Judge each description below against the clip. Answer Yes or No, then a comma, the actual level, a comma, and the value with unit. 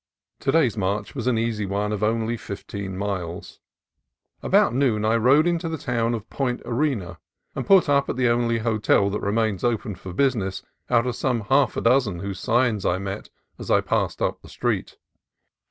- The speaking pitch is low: Yes, low, 115 Hz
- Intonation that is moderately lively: Yes, average, 4.0 semitones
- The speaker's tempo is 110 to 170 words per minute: No, average, 185 wpm